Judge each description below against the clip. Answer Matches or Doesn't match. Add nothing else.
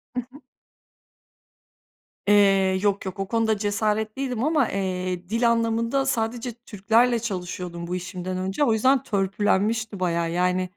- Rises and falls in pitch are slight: Doesn't match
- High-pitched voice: Matches